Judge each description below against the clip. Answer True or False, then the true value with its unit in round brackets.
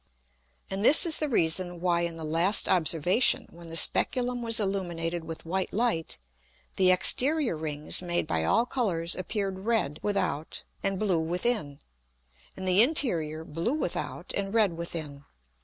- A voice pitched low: False (180 Hz)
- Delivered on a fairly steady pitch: False (4.8 semitones)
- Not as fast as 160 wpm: True (150 wpm)